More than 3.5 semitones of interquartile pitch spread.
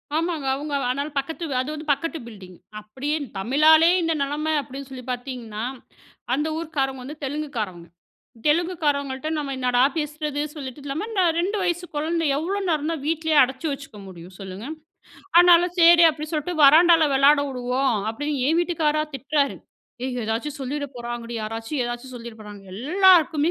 Yes: average, 4.1 semitones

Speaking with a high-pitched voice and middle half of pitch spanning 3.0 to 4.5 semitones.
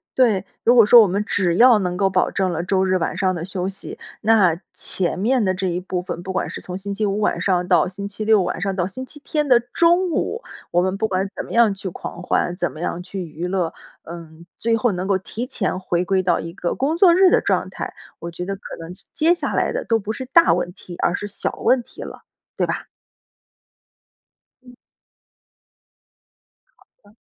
Yes: high, 195 Hz; average, 4.1 semitones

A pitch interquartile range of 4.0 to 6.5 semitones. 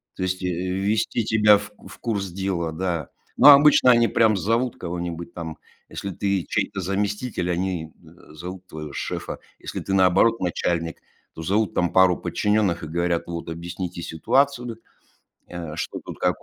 No: average, 3.4 semitones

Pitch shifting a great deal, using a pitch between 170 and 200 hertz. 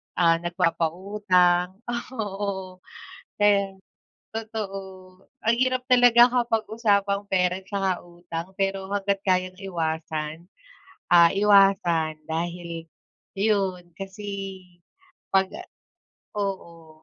No: average, 2.7 semitones; high, 190 Hz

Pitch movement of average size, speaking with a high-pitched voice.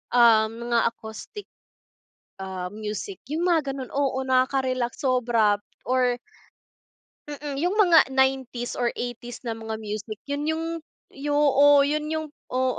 Yes: average, 3.7 semitones; very high, 255 Hz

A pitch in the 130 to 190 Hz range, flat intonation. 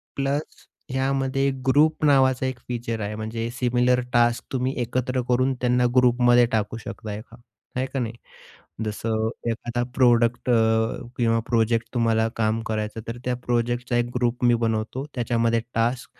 No: low, 120 Hz; narrow, 1.9 semitones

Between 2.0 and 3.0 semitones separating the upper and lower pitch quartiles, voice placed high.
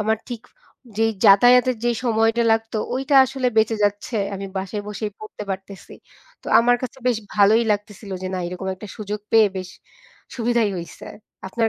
Yes: average, 2.7 semitones; high, 220 Hz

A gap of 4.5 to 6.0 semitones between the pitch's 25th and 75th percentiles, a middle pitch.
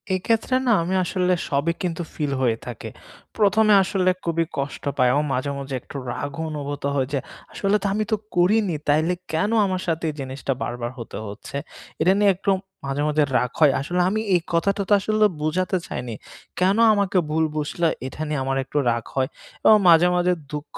Yes: average, 5.2 semitones; medium, 165 Hz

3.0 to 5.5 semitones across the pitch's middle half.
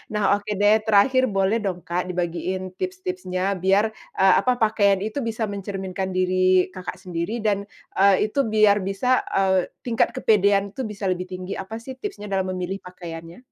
No: narrow, 2.4 semitones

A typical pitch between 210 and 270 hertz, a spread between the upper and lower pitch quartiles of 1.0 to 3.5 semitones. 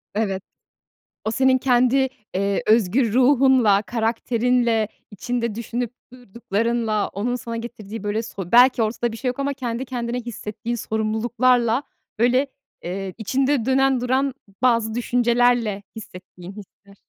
Yes: high, 235 Hz; narrow, 2.5 semitones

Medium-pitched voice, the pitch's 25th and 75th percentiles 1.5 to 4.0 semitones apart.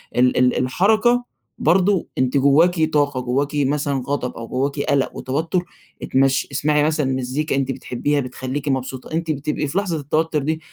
Yes: medium, 145 Hz; average, 3.2 semitones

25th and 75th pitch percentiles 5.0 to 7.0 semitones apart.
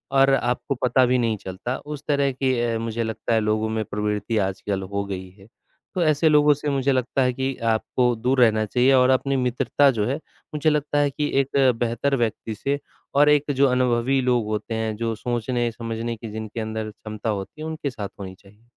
No: average, 3.7 semitones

